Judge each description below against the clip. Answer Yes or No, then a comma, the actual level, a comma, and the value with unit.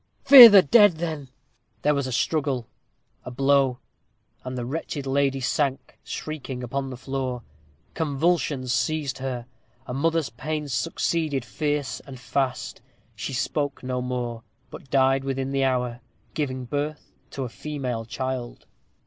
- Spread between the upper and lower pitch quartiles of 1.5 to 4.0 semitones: Yes, average, 2.7 semitones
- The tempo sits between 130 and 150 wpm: Yes, average, 140 wpm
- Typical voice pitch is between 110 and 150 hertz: Yes, low, 135 Hz